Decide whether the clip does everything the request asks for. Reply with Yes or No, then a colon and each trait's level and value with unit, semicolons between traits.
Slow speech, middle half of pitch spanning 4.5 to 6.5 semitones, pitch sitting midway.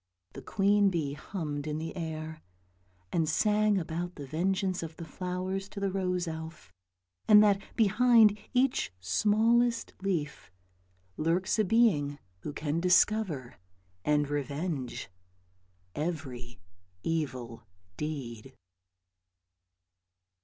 Yes: slow, 105 wpm; average, 5.1 semitones; medium, 165 Hz